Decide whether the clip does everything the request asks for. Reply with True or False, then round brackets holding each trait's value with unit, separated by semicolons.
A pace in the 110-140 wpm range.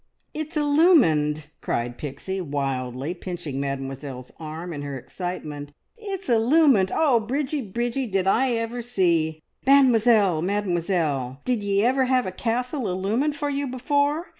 True (135 wpm)